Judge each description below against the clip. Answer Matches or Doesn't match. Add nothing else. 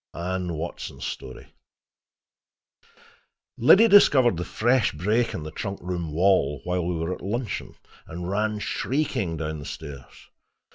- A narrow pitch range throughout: Doesn't match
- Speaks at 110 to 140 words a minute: Matches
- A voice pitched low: Matches